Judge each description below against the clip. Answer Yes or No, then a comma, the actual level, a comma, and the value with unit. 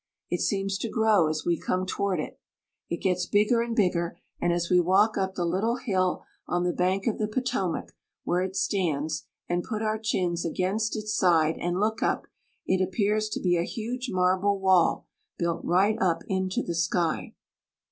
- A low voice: No, high, 190 Hz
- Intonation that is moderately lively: Yes, average, 3.4 semitones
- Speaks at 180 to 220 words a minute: Yes, average, 190 wpm